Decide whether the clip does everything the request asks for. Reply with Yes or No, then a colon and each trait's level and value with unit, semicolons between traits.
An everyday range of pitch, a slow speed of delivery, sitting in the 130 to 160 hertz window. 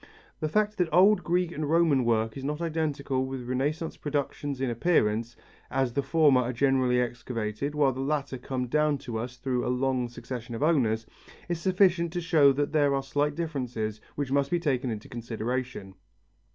No: average, 3.7 semitones; average, 180 wpm; low, 135 Hz